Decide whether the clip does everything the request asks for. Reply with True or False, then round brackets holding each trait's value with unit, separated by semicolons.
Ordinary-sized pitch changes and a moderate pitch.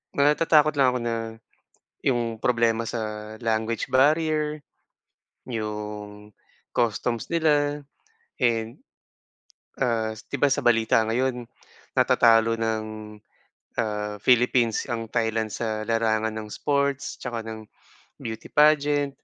False (3.7 semitones; 115 Hz)